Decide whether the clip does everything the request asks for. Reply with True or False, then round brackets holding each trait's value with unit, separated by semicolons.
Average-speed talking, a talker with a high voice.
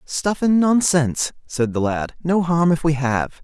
False (190 wpm; 155 Hz)